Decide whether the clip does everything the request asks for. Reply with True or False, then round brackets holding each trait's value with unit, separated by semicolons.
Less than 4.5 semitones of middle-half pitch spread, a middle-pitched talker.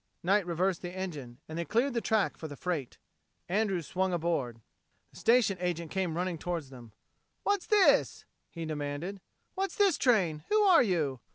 False (4.9 semitones; 180 Hz)